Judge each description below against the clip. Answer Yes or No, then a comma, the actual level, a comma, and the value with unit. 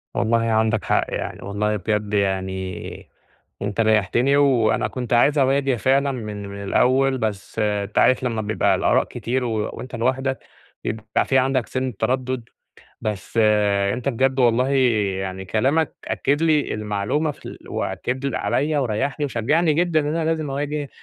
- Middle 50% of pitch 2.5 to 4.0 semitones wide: No, average, 4.4 semitones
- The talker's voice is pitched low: Yes, low, 120 Hz